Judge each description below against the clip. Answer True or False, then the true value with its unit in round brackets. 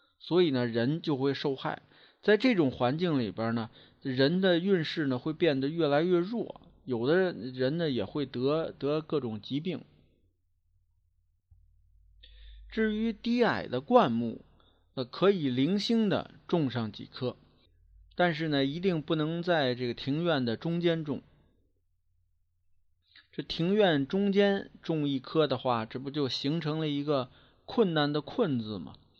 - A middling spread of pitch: False (7.6 semitones)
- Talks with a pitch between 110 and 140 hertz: True (135 Hz)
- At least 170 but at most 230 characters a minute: True (200 characters per minute)